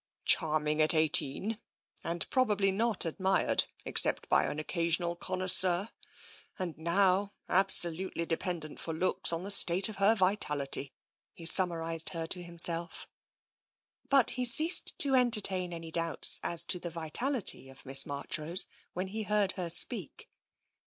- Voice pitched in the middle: Yes, medium, 175 Hz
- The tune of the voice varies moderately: Yes, average, 3.3 semitones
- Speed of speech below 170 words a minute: Yes, average, 150 wpm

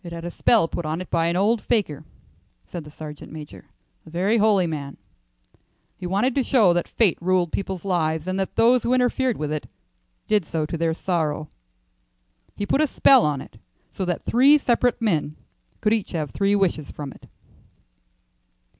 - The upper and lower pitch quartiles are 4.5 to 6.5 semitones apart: Yes, wide, 5.6 semitones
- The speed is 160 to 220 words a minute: Yes, average, 185 wpm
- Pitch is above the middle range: No, medium, 180 Hz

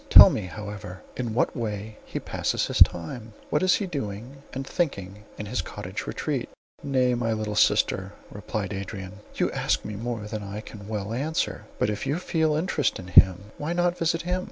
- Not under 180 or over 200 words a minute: Yes, average, 190 wpm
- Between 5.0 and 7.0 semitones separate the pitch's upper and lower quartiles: Yes, wide, 5.4 semitones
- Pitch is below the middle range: Yes, low, 110 Hz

